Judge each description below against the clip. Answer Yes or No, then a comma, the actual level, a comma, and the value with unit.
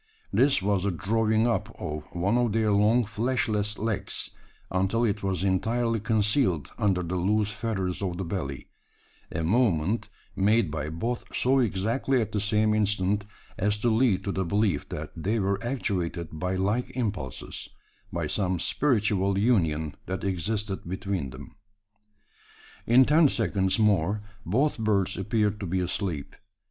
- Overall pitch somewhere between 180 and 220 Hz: No, low, 100 Hz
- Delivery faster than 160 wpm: No, average, 150 wpm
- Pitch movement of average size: Yes, average, 3.4 semitones